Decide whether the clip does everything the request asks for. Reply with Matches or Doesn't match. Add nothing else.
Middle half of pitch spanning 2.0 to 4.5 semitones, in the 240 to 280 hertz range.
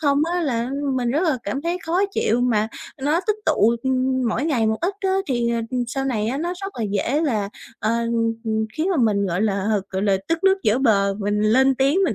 Doesn't match